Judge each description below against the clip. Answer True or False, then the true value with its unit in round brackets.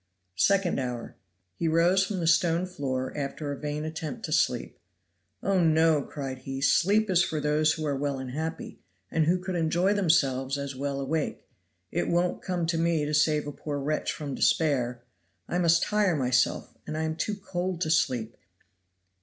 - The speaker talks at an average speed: True (180 wpm)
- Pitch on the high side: False (155 Hz)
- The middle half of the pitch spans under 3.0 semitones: False (3.7 semitones)